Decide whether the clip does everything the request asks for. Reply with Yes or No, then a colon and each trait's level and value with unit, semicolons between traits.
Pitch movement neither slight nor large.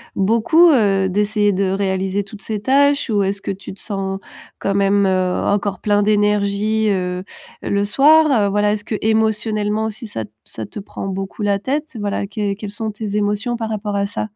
No: narrow, 1.7 semitones